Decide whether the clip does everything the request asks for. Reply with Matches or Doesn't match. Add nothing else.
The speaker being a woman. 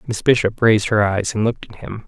Doesn't match